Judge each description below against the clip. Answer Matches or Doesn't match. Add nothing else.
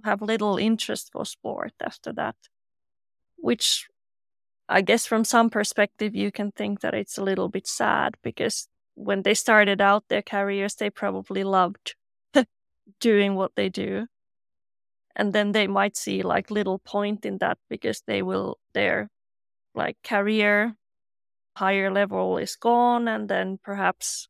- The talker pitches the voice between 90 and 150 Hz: Doesn't match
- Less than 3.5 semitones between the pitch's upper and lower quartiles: Matches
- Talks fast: Doesn't match